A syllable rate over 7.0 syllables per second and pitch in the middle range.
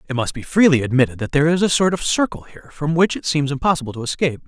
Yes: 7.4 syllables/s; medium, 150 Hz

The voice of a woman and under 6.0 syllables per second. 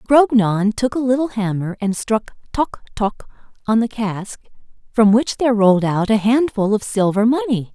Yes: female; 4.7 syllables/s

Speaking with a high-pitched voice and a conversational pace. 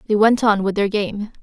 No: high, 210 Hz; fast, 255 wpm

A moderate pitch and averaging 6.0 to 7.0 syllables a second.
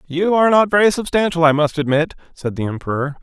Yes: medium, 165 Hz; 6.4 syllables/s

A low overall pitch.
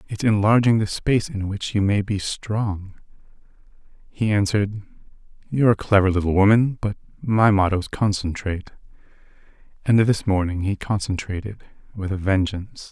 Yes: low, 100 Hz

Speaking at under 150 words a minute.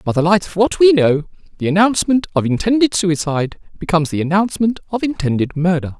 No: average, 180 wpm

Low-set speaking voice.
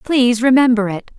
No: high, 240 Hz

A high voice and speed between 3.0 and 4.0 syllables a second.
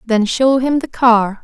Yes: high, 240 Hz; 3.8 syllables/s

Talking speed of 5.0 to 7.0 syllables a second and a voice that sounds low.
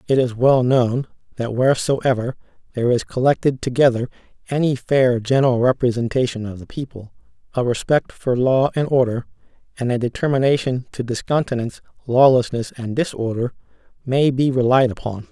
Yes: 5.5 syllables/s; low, 125 Hz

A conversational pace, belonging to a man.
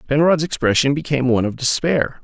Yes: average, 160 wpm; male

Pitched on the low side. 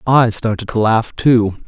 Yes: low, 115 Hz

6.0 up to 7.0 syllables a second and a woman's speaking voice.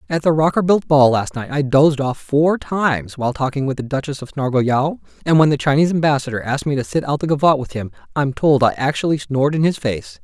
No: 6.2 syllables/s; male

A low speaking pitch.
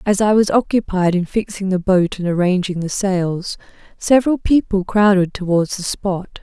No: high, 190 Hz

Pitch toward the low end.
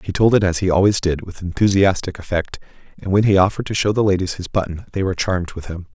Yes: very low, 95 Hz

